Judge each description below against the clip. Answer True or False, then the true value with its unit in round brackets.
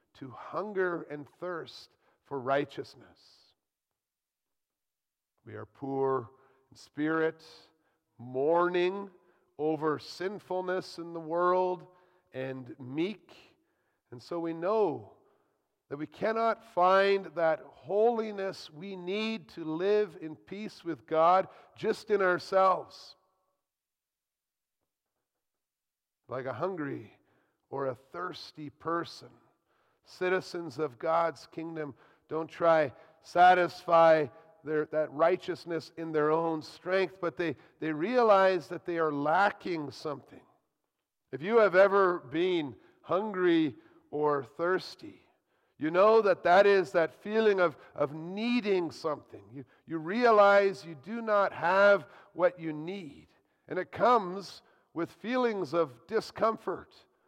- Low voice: False (175 Hz)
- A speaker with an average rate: False (110 wpm)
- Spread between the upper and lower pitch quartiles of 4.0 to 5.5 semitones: False (3.6 semitones)